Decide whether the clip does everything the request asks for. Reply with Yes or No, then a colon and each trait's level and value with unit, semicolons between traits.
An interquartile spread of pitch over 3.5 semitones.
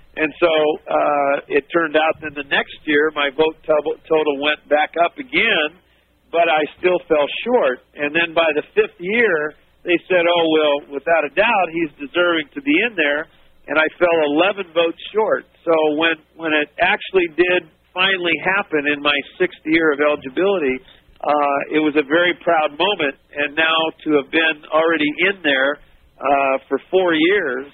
No: average, 2.8 semitones